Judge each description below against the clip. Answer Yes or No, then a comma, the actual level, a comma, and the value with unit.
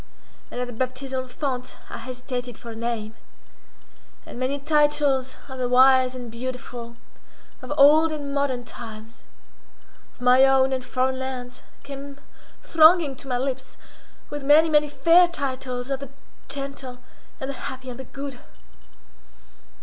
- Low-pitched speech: No, very high, 260 Hz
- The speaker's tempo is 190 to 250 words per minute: No, average, 145 wpm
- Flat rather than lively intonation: Yes, narrow, 2.0 semitones